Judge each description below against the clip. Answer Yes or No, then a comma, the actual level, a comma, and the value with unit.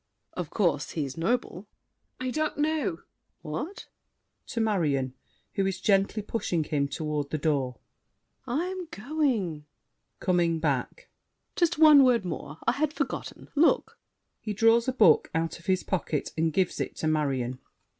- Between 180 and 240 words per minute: No, average, 155 wpm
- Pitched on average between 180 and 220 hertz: Yes, high, 190 Hz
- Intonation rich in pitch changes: Yes, wide, 8.8 semitones